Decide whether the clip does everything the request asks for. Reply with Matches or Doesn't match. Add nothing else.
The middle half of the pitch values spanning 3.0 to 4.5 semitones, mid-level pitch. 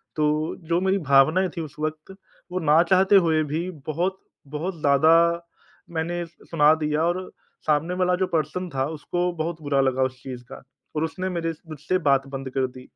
Matches